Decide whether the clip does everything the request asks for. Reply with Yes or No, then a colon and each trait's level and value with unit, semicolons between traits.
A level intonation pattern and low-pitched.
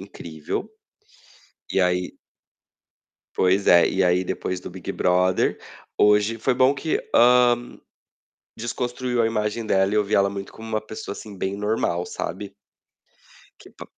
No: average, 3.9 semitones; low, 105 Hz